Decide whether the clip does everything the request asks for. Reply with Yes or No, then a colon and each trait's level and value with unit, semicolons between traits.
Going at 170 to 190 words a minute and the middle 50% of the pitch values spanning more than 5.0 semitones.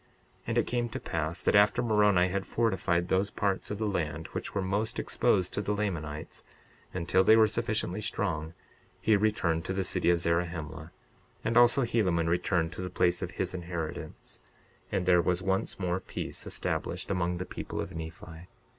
No: average, 180 wpm; average, 3.3 semitones